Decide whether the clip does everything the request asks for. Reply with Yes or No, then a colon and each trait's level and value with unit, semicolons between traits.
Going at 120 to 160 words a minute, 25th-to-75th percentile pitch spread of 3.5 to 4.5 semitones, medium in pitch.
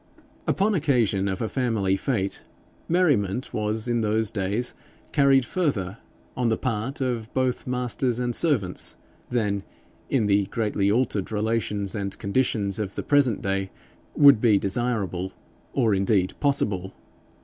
No: slow, 135 wpm; average, 4.2 semitones; low, 110 Hz